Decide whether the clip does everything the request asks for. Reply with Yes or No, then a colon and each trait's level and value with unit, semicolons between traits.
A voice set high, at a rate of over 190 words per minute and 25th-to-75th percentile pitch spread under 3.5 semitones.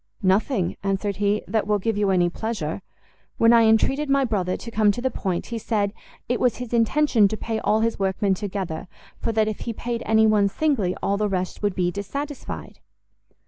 Yes: high, 215 Hz; average, 200 wpm; average, 2.8 semitones